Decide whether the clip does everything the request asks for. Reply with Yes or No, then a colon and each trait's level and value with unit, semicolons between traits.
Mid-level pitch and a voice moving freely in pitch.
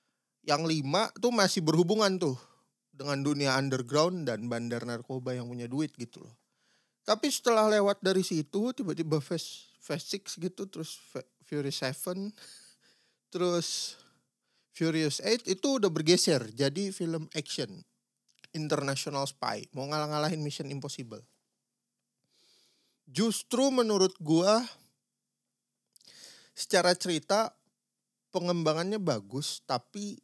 Yes: medium, 160 Hz; wide, 5.9 semitones